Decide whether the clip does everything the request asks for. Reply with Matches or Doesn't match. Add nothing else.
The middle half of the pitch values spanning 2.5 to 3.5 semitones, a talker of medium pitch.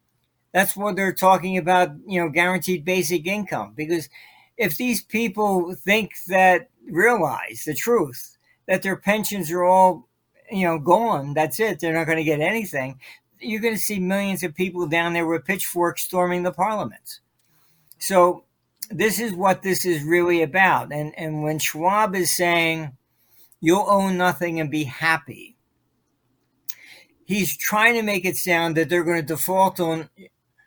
Matches